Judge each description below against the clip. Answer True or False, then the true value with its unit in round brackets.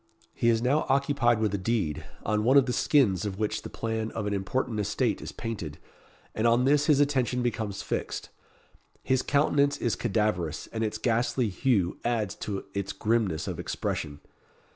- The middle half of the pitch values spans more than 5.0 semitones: False (4.0 semitones)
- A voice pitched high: False (115 Hz)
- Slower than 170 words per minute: False (175 wpm)